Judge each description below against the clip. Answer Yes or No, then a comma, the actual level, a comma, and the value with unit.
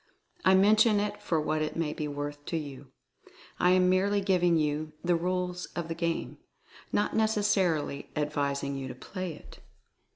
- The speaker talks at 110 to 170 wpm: Yes, average, 165 wpm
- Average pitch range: Yes, average, 4.0 semitones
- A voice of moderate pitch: Yes, medium, 170 Hz